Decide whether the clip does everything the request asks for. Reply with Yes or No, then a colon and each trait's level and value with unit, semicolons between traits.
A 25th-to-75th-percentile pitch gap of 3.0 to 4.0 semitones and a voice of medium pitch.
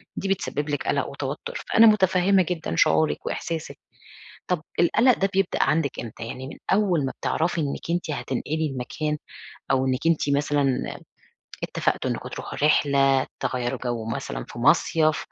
No: average, 4.8 semitones; medium, 155 Hz